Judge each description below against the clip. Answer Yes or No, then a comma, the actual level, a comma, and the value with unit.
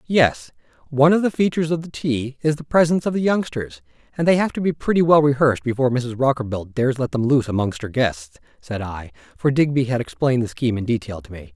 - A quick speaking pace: Yes, fast, 230 wpm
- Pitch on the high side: No, low, 130 Hz